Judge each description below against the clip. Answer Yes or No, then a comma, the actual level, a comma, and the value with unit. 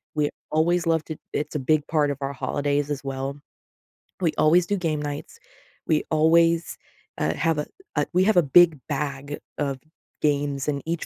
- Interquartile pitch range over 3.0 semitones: No, narrow, 2.5 semitones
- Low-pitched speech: No, medium, 150 Hz